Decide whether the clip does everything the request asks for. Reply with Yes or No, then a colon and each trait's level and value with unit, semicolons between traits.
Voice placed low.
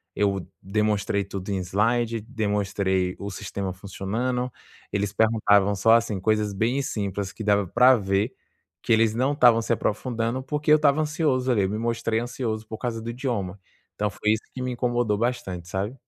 Yes: low, 110 Hz